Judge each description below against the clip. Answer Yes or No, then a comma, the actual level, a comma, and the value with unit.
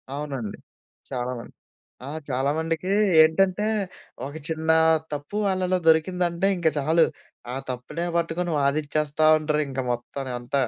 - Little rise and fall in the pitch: No, average, 3.5 semitones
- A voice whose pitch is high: No, medium, 155 Hz